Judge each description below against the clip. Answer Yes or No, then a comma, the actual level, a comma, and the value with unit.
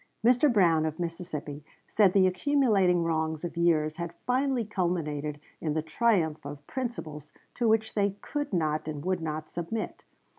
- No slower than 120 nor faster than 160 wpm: Yes, average, 155 wpm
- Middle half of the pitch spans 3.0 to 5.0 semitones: No, wide, 5.6 semitones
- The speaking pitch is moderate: Yes, medium, 170 Hz